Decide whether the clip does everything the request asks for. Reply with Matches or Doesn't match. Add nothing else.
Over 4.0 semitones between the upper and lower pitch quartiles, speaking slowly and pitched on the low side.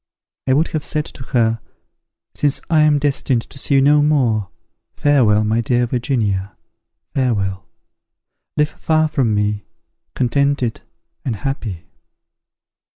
Matches